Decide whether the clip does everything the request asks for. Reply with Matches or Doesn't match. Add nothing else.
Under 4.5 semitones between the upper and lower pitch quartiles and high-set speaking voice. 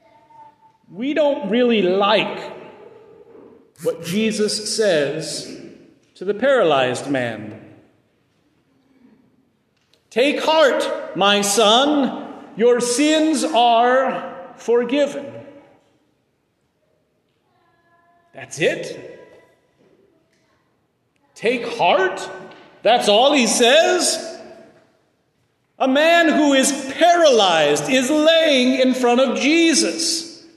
Doesn't match